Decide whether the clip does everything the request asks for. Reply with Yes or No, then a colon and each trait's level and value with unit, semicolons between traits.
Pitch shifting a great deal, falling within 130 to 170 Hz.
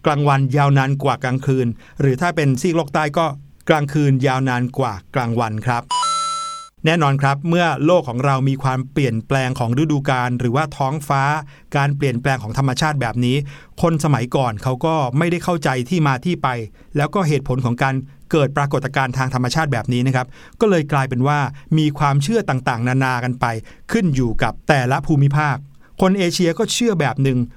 No: average, 3.5 semitones; medium, 140 Hz